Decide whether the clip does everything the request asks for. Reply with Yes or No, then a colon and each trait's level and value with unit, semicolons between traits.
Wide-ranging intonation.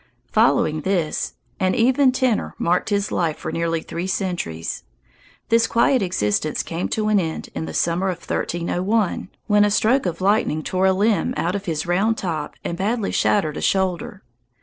No: average, 4.0 semitones